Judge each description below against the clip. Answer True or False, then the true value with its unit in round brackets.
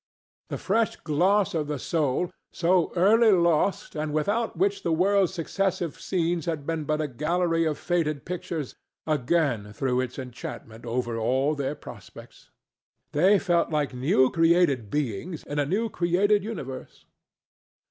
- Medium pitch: True (160 Hz)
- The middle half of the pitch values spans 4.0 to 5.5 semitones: True (4.4 semitones)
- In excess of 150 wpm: False (145 wpm)